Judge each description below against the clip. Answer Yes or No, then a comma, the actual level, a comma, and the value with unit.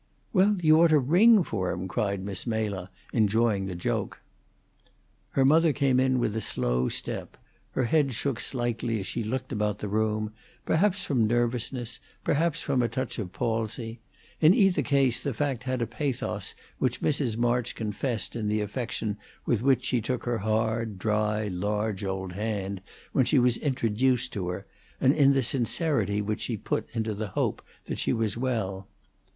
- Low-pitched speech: Yes, low, 115 Hz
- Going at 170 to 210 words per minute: Yes, average, 175 wpm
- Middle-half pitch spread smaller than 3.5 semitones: No, average, 4.0 semitones